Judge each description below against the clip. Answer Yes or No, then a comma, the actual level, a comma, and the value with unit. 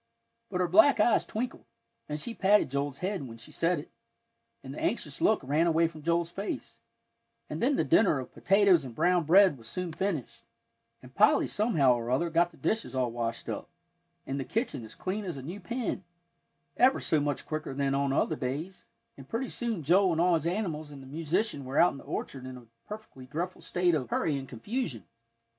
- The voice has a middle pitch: Yes, medium, 165 Hz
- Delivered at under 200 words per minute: No, fast, 205 wpm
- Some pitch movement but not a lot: No, wide, 6.0 semitones